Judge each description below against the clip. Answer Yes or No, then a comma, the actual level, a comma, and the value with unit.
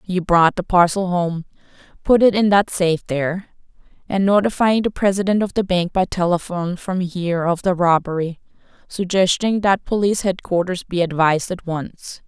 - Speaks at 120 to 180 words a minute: Yes, average, 155 wpm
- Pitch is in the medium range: Yes, medium, 180 Hz